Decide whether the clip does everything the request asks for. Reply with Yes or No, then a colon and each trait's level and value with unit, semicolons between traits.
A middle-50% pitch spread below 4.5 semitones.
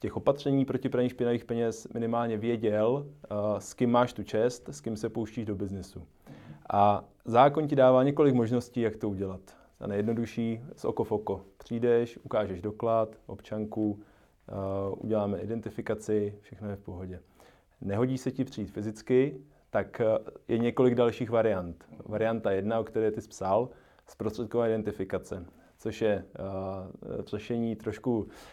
Yes: average, 2.7 semitones